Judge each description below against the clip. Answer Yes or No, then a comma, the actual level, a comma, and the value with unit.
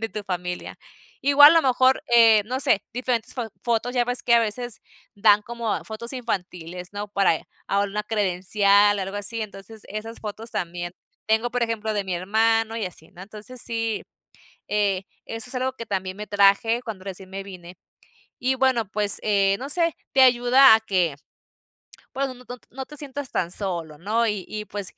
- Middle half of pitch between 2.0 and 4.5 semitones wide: Yes, average, 3.5 semitones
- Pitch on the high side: Yes, high, 215 Hz